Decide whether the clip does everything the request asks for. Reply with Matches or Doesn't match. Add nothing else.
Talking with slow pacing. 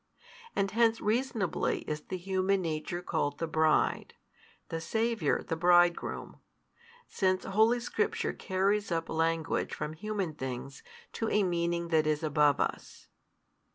Matches